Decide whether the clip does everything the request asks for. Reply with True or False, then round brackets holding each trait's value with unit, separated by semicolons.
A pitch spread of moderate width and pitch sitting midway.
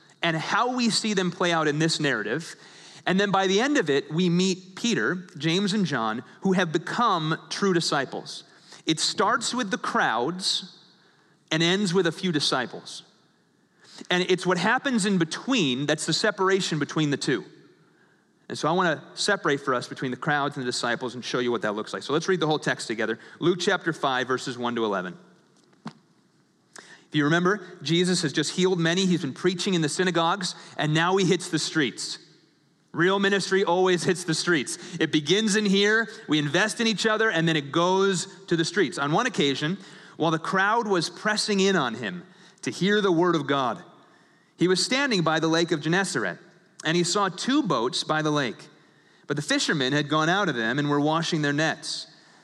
True (3.7 semitones; 175 Hz)